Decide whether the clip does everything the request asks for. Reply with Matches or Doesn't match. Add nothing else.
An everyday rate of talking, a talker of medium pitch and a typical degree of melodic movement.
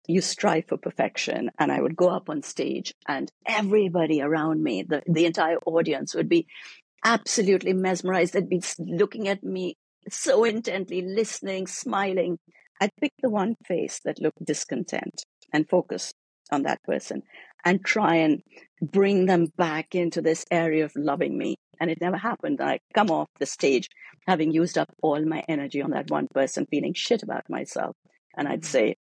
Matches